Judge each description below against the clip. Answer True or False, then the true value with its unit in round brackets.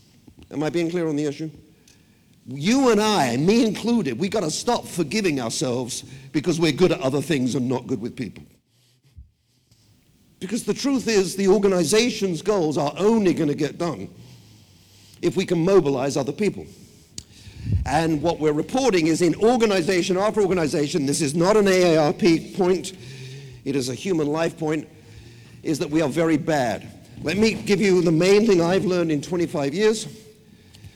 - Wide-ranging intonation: True (6.2 semitones)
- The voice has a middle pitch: True (160 Hz)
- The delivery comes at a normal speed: True (170 wpm)